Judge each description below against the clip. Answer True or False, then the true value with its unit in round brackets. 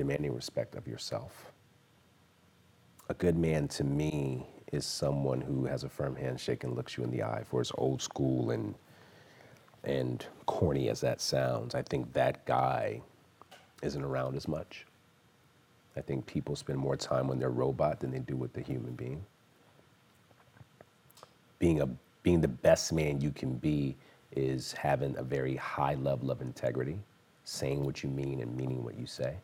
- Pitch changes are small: True (1.5 semitones)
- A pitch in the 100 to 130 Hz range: False (65 Hz)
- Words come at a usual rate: True (165 wpm)